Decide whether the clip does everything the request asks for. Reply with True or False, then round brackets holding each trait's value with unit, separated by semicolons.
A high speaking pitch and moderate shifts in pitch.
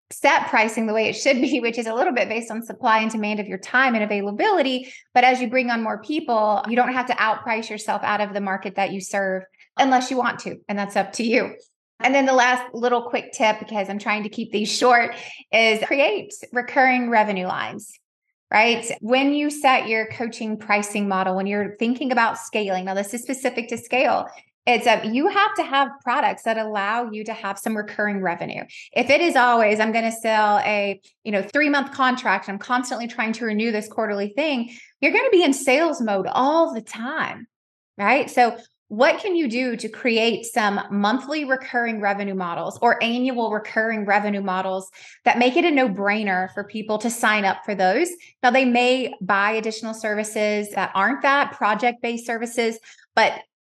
True (225 Hz; 3.4 semitones)